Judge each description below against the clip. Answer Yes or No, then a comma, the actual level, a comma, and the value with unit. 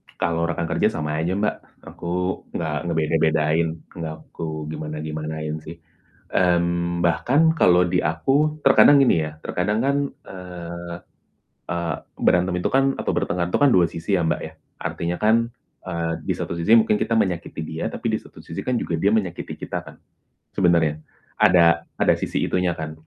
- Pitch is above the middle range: No, very low, 85 Hz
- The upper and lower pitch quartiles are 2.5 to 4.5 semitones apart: Yes, average, 2.9 semitones